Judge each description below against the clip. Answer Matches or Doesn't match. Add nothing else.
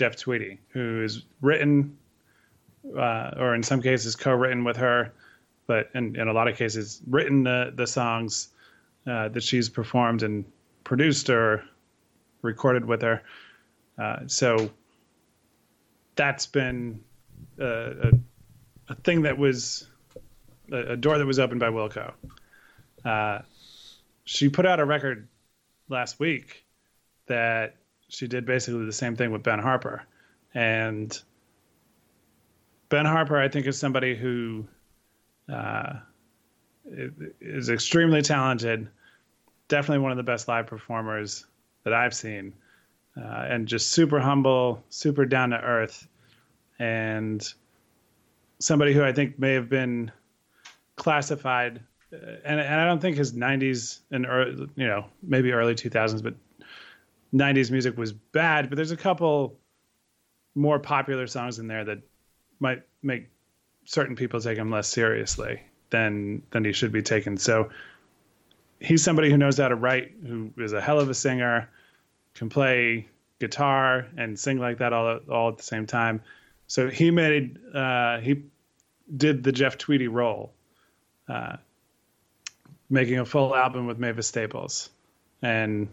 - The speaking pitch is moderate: Doesn't match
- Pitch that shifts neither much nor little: Matches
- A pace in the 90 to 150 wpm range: Matches